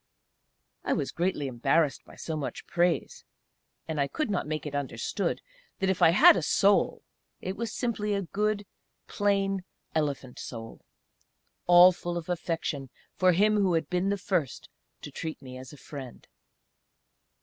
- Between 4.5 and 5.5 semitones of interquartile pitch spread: Yes, average, 5.1 semitones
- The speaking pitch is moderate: Yes, medium, 175 Hz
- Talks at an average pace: Yes, average, 160 wpm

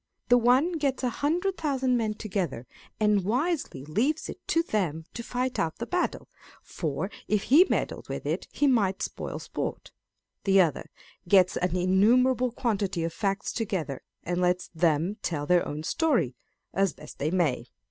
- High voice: Yes, high, 200 Hz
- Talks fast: No, average, 165 wpm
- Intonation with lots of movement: Yes, wide, 6.4 semitones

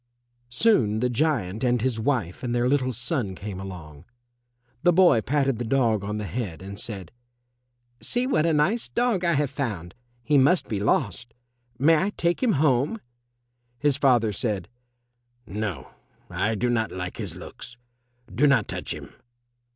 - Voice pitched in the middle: No, low, 120 Hz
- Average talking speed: Yes, average, 160 wpm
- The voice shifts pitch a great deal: Yes, wide, 5.8 semitones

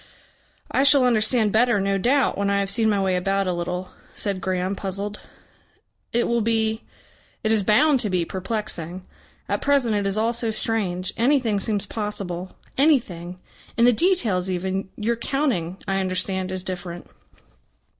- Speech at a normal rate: Yes, average, 160 wpm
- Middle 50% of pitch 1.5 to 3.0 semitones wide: No, average, 3.7 semitones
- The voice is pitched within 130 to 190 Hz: No, high, 200 Hz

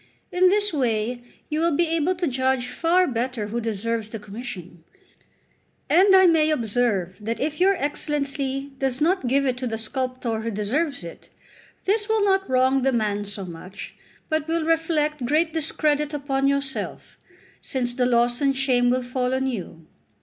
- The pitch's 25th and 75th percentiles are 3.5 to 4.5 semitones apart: No, average, 4.9 semitones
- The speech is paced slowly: No, average, 170 wpm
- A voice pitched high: Yes, very high, 265 Hz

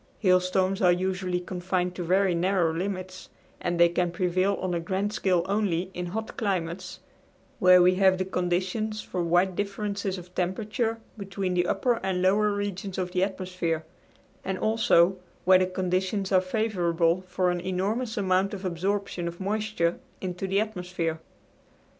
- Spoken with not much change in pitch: Yes, narrow, 1.9 semitones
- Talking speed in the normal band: Yes, average, 155 wpm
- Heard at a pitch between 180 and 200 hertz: Yes, medium, 185 Hz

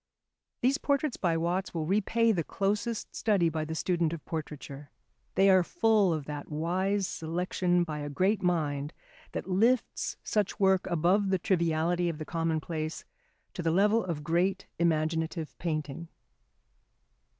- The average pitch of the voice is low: No, medium, 175 Hz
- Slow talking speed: No, average, 145 wpm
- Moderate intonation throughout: Yes, average, 3.5 semitones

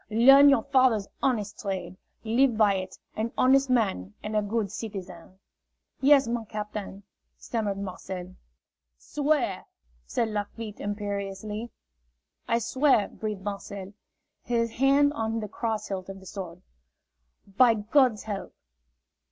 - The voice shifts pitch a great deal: No, average, 3.3 semitones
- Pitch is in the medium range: No, high, 215 Hz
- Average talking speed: No, slow, 125 wpm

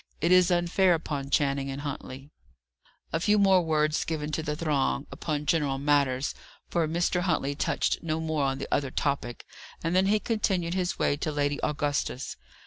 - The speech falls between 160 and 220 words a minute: Yes, average, 175 wpm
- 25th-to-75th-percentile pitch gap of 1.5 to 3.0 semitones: No, average, 3.4 semitones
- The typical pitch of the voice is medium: Yes, medium, 155 Hz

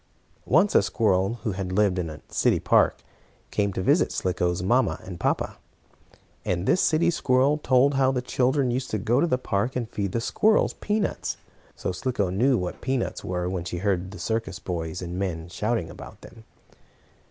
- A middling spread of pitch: No, wide, 5.9 semitones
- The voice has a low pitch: Yes, low, 105 Hz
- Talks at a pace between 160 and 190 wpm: Yes, average, 185 wpm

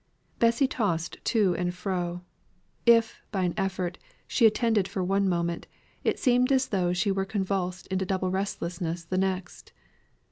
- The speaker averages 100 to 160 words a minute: Yes, average, 150 wpm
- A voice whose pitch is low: No, high, 190 Hz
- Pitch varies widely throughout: No, average, 2.9 semitones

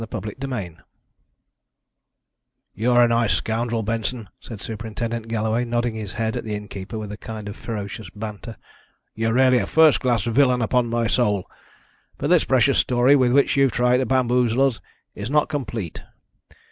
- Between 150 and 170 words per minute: Yes, average, 160 wpm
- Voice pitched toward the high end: No, low, 115 Hz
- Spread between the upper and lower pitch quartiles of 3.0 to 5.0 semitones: No, narrow, 2.5 semitones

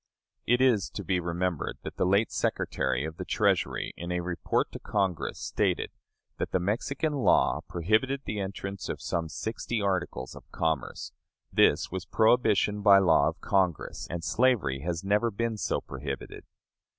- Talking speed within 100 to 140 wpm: No, average, 160 wpm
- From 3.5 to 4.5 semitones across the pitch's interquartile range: Yes, average, 4.2 semitones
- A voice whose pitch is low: Yes, very low, 95 Hz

